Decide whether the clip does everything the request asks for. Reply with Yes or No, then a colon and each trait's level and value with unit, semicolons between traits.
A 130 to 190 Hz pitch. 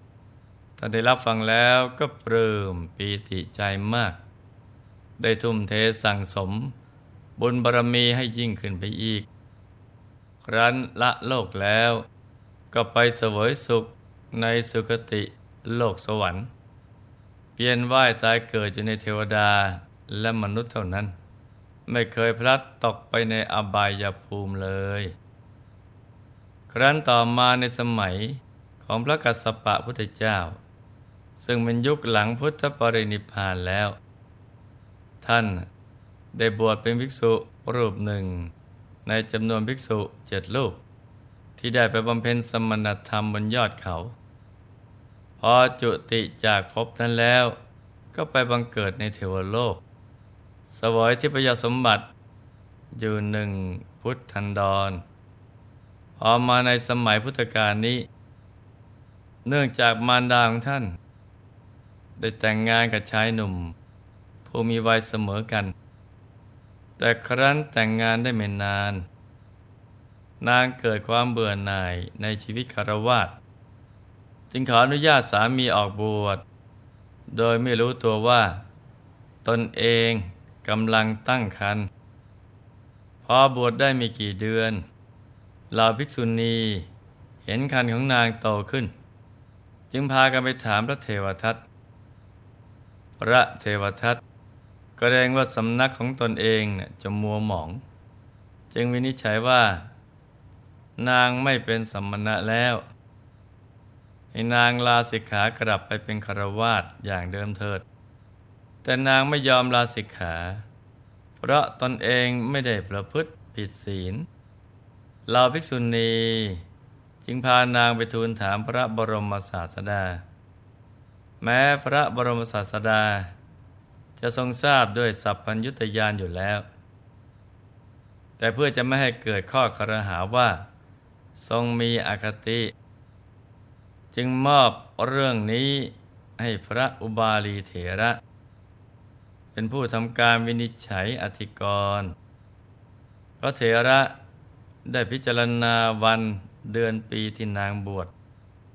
No: low, 110 Hz